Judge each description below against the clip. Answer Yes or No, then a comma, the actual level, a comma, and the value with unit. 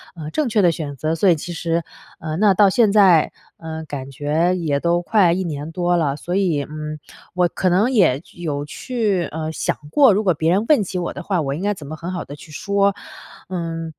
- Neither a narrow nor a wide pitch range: Yes, average, 3.6 semitones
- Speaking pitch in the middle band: Yes, medium, 170 Hz